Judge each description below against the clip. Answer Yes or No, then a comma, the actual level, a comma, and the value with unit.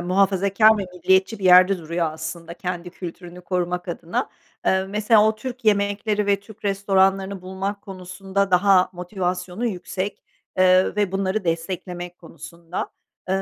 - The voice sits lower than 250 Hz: Yes, high, 190 Hz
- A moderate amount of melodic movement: No, narrow, 2.0 semitones